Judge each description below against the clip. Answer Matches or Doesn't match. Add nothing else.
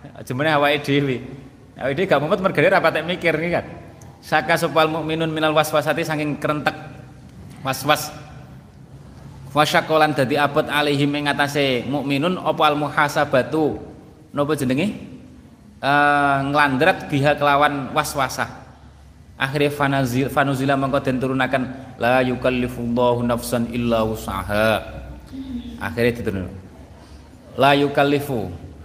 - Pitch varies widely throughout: Doesn't match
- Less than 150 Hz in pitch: Matches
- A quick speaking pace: Doesn't match